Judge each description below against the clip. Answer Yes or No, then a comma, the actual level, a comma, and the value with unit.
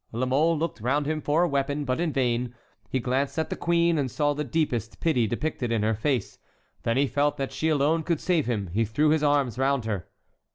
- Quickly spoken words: Yes, fast, 230 wpm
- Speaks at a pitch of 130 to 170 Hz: Yes, medium, 140 Hz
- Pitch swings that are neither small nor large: Yes, average, 4.1 semitones